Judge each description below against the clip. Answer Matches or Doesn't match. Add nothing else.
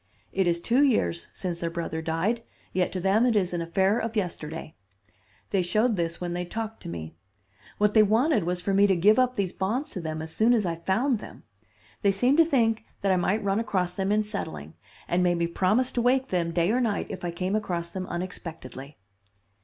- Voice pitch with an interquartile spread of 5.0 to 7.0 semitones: Doesn't match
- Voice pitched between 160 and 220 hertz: Matches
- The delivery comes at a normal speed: Doesn't match